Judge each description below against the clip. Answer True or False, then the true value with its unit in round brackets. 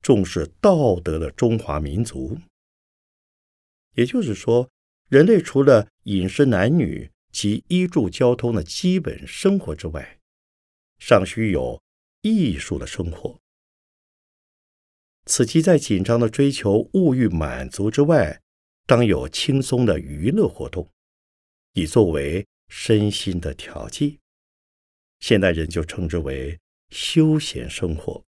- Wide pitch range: True (8.9 semitones)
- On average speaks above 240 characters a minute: False (175 characters per minute)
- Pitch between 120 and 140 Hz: False (105 Hz)